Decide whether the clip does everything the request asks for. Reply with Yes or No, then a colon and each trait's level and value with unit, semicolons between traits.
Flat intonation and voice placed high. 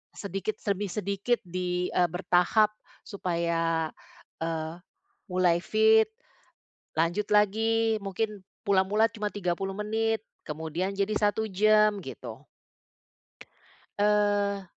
No: average, 3.0 semitones; high, 200 Hz